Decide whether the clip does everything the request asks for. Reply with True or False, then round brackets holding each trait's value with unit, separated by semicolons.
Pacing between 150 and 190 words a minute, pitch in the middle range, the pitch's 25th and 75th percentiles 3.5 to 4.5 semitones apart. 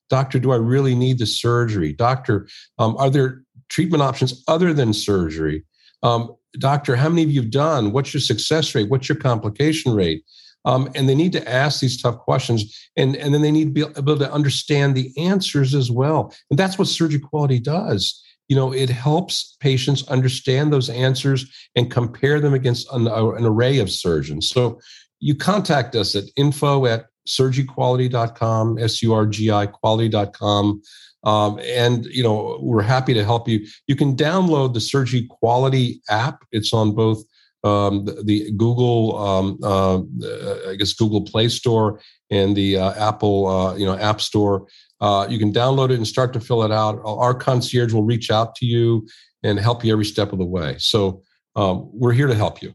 False (185 wpm; 120 Hz; 4.2 semitones)